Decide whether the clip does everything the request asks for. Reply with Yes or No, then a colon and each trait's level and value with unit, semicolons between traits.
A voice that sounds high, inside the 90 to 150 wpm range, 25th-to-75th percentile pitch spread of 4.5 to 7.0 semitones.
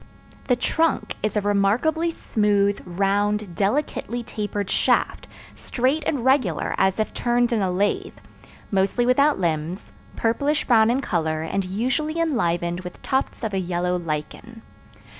Yes: high, 210 Hz; average, 140 wpm; average, 5.2 semitones